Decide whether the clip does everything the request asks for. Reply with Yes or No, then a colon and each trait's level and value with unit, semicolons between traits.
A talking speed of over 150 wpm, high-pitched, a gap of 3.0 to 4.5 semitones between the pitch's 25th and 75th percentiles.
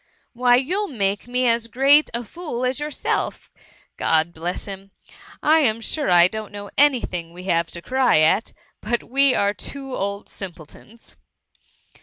No: average, 160 wpm; high, 230 Hz; wide, 5.6 semitones